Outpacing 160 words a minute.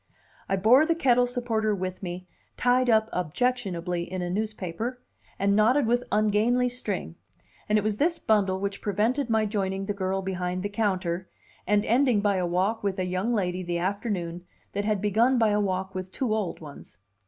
Yes: average, 180 wpm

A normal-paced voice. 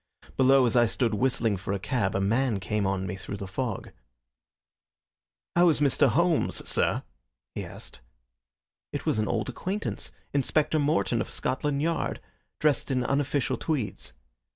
Yes: average, 155 wpm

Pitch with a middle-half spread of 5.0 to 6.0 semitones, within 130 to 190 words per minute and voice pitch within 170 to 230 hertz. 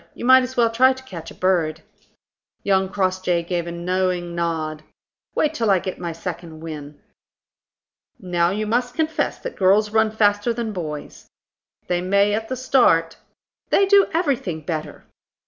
Yes: wide, 5.4 semitones; average, 160 wpm; high, 190 Hz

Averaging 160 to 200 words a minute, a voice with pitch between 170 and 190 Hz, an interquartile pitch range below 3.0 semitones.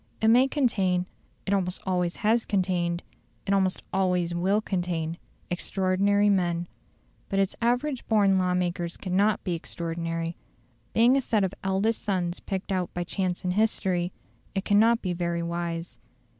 No: average, 150 wpm; medium, 185 Hz; narrow, 2.6 semitones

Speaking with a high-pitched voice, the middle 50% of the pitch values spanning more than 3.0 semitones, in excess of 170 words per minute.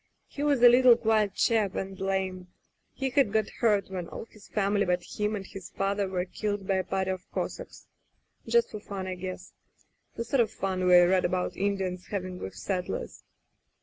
No: high, 195 Hz; average, 2.7 semitones; average, 195 wpm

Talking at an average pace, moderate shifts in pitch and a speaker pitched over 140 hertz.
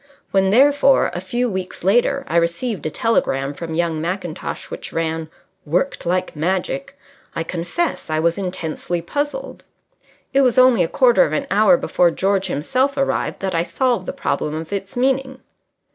No: average, 165 wpm; wide, 7.3 semitones; high, 190 Hz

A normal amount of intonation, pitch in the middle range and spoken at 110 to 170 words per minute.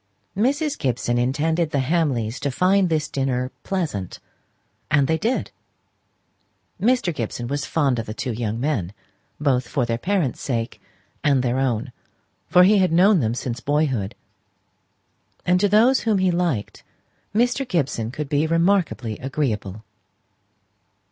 No: wide, 6.8 semitones; medium, 145 Hz; average, 140 wpm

